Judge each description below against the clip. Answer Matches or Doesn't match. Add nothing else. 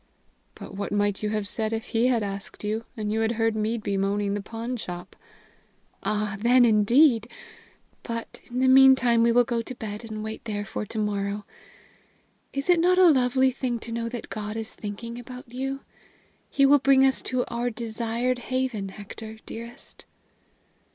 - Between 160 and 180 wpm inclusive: Matches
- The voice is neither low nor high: Doesn't match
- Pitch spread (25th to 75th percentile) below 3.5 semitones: Matches